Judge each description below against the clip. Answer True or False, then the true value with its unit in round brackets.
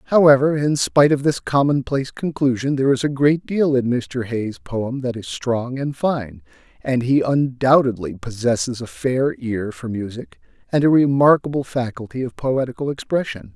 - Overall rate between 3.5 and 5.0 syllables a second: True (4.8 syllables/s)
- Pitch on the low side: True (130 Hz)